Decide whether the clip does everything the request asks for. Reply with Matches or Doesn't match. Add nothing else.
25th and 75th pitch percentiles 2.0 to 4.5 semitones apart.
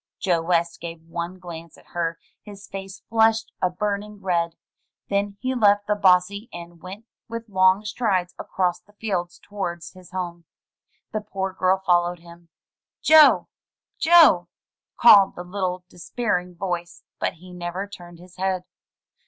Matches